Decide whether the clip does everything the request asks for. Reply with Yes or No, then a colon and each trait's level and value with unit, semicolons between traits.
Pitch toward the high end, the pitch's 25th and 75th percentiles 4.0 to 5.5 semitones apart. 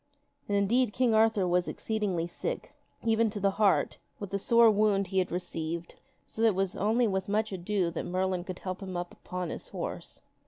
No: high, 195 Hz; average, 3.2 semitones